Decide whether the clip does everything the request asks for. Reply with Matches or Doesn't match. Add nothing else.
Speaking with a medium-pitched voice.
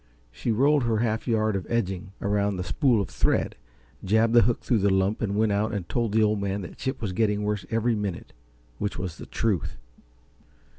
Doesn't match